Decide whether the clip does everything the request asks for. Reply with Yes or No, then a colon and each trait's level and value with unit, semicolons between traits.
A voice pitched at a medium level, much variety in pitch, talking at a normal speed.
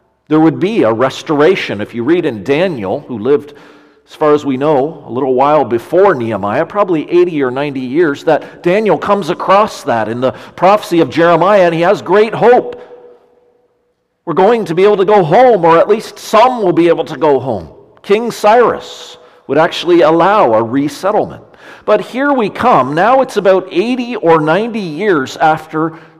Yes: medium, 175 Hz; wide, 5.9 semitones; average, 180 wpm